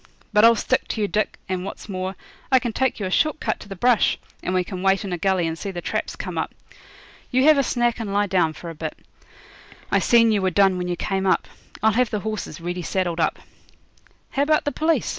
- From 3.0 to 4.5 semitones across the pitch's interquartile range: Yes, average, 4.2 semitones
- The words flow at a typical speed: No, fast, 245 wpm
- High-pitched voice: Yes, high, 195 Hz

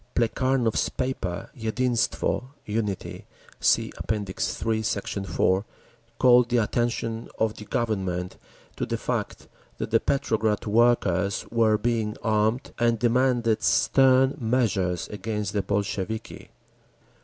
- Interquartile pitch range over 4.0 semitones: No, narrow, 2.5 semitones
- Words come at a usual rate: No, slow, 110 wpm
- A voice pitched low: Yes, low, 110 Hz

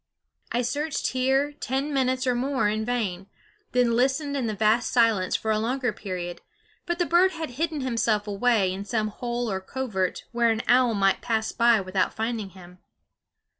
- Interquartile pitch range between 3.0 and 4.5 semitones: Yes, average, 3.8 semitones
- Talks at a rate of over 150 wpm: Yes, average, 175 wpm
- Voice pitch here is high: Yes, high, 235 Hz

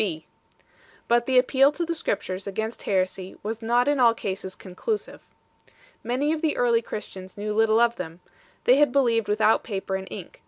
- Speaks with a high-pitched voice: Yes, high, 225 Hz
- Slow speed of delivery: No, average, 185 wpm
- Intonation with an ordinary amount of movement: Yes, average, 4.5 semitones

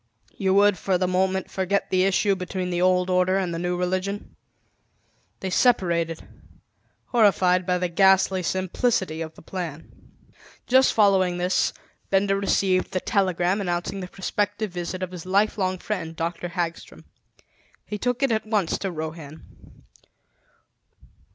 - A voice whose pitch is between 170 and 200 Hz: Yes, medium, 185 Hz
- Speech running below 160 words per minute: Yes, average, 140 wpm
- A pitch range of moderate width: No, narrow, 1.9 semitones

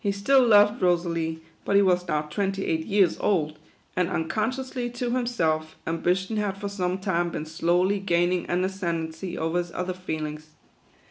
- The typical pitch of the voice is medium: Yes, medium, 180 Hz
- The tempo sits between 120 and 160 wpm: No, average, 170 wpm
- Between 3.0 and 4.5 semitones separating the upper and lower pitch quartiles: Yes, average, 3.5 semitones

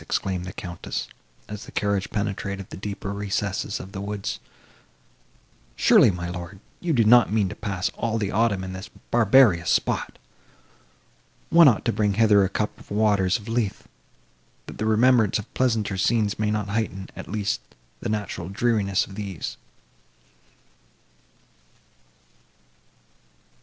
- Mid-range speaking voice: No, low, 105 Hz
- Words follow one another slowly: No, average, 145 wpm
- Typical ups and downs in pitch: No, narrow, 2.3 semitones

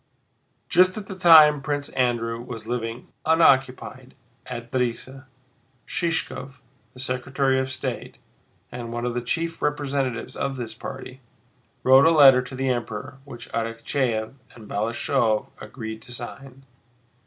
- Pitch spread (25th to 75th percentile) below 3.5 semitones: Yes, average, 2.8 semitones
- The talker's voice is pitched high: No, low, 130 Hz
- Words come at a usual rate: No, slow, 130 wpm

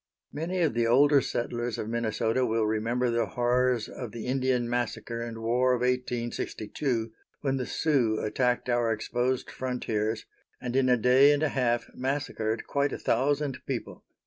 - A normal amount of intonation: No, narrow, 2.0 semitones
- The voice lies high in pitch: No, low, 125 Hz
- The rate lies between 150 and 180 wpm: Yes, average, 160 wpm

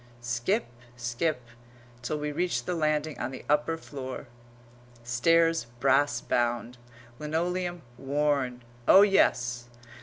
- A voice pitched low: No, medium, 145 Hz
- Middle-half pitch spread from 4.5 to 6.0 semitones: Yes, average, 5.0 semitones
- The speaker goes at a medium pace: No, slow, 110 wpm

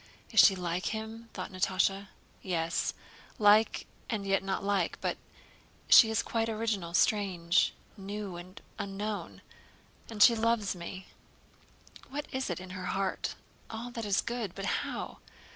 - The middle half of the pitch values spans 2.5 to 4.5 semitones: Yes, average, 3.1 semitones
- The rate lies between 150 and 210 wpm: No, average, 140 wpm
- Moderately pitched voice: No, high, 200 Hz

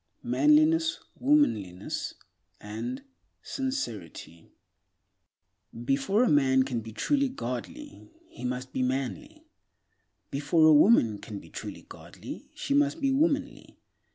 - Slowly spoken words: Yes, slow, 110 wpm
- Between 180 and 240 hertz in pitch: No, medium, 150 Hz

